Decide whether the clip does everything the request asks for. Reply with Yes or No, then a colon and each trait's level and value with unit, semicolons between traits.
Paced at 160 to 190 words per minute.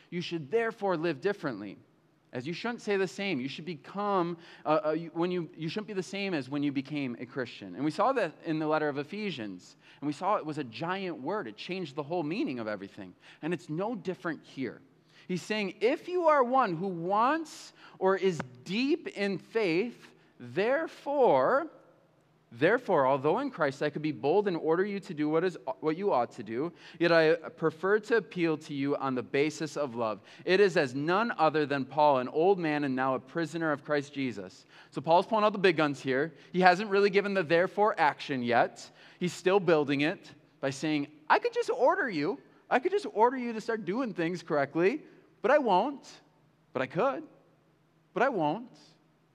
No: fast, 205 wpm